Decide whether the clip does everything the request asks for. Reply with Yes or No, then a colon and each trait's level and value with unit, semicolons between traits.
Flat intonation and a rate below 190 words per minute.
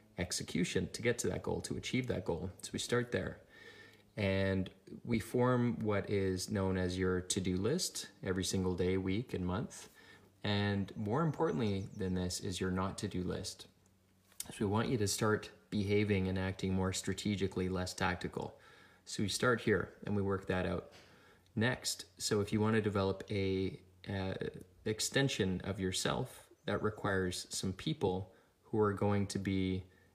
Yes: narrow, 2.1 semitones; average, 165 wpm